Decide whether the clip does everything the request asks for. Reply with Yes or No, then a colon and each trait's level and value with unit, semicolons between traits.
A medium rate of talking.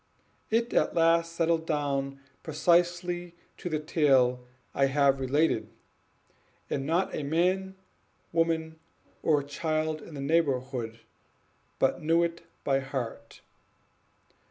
No: slow, 110 wpm